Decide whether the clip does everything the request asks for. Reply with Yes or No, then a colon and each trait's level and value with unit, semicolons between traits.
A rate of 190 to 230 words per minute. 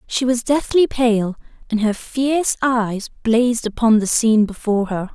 No: average, 165 wpm